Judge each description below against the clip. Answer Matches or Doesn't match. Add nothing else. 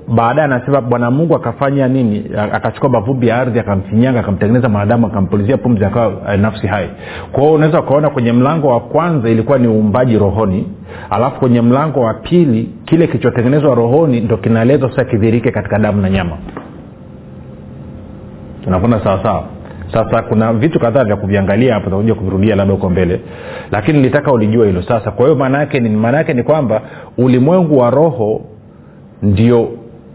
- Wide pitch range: Doesn't match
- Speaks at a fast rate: Doesn't match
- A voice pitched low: Matches